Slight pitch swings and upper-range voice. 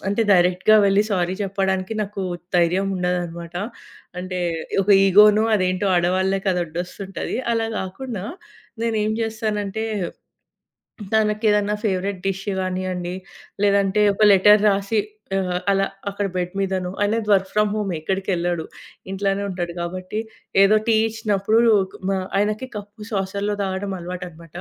Yes: narrow, 2.2 semitones; high, 195 Hz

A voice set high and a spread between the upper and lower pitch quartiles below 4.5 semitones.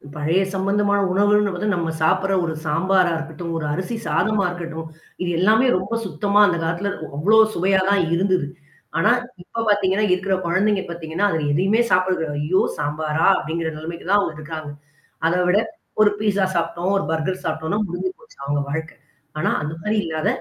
No: medium, 180 Hz; average, 3.8 semitones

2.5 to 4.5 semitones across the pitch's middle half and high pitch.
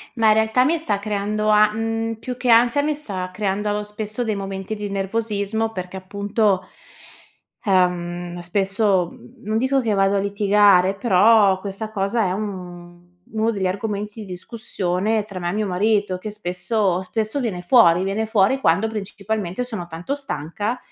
Yes: average, 2.8 semitones; high, 205 Hz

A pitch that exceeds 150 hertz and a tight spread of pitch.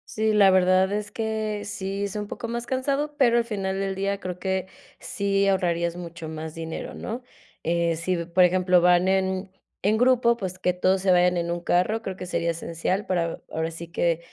No: high, 190 Hz; average, 3.1 semitones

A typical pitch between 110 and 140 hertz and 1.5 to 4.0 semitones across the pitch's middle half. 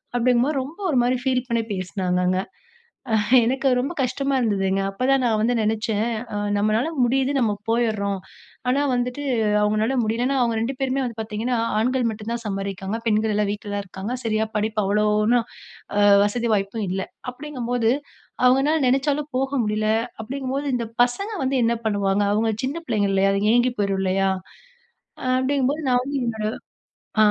No: high, 230 Hz; average, 3.7 semitones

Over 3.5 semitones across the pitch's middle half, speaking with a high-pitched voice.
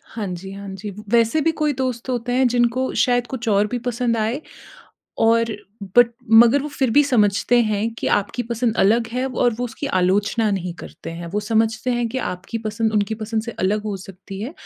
No: average, 2.9 semitones; high, 225 Hz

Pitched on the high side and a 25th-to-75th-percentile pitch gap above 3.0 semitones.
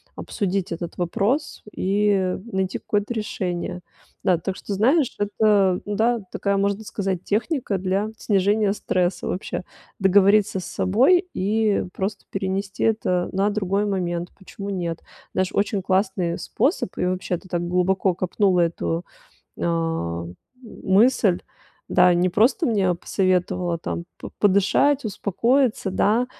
No: high, 195 Hz; narrow, 2.5 semitones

